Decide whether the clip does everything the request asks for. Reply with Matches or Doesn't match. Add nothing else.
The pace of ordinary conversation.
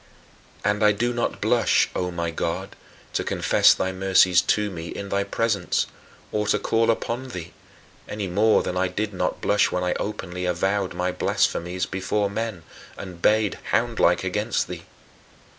Matches